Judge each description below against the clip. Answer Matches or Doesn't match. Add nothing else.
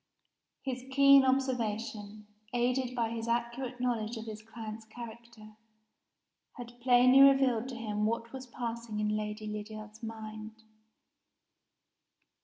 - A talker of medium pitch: Doesn't match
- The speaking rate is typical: Doesn't match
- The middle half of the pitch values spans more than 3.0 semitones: Doesn't match